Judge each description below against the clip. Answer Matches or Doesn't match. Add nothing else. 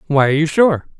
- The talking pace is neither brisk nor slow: Doesn't match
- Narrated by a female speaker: Doesn't match